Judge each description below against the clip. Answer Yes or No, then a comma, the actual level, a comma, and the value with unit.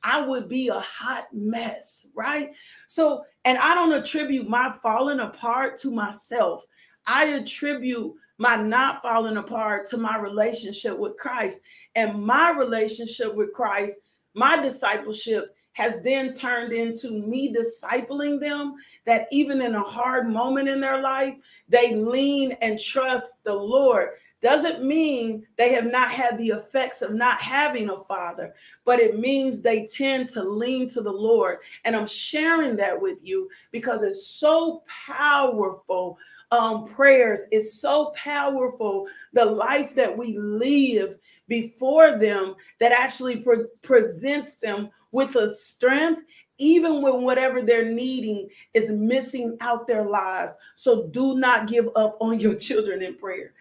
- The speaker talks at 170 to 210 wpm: No, average, 145 wpm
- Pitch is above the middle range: Yes, very high, 250 Hz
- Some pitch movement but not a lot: Yes, average, 4.1 semitones